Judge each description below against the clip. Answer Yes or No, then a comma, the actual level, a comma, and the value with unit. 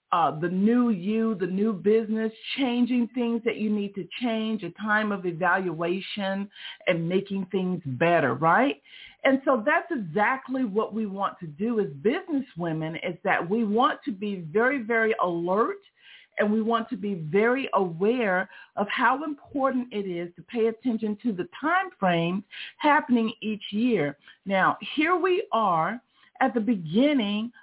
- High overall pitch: Yes, high, 215 Hz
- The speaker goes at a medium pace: Yes, average, 155 wpm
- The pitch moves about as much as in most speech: Yes, average, 4.6 semitones